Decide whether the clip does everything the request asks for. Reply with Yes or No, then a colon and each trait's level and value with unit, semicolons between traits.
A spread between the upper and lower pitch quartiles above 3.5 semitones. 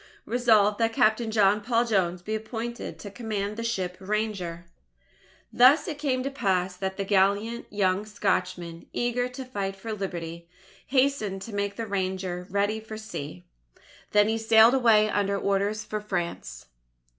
No: average, 3.0 semitones